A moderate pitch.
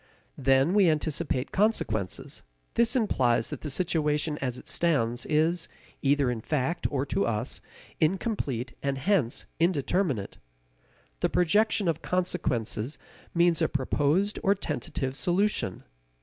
Yes: medium, 150 Hz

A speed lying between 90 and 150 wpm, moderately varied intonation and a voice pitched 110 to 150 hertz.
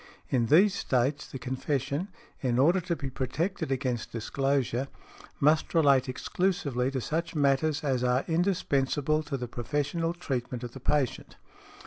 Yes: average, 140 wpm; average, 3.7 semitones; medium, 140 Hz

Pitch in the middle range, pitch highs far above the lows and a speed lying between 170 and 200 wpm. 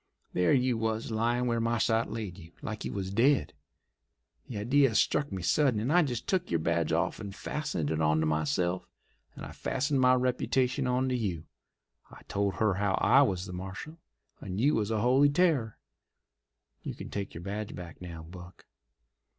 No: low, 110 Hz; wide, 5.8 semitones; average, 180 wpm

